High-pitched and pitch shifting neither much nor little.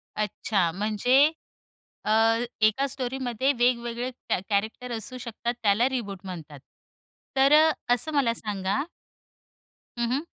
Yes: high, 235 Hz; average, 3.9 semitones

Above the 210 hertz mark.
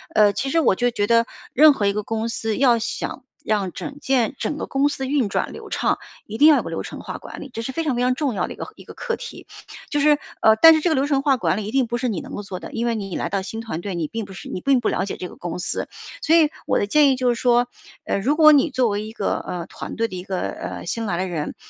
Yes: high, 235 Hz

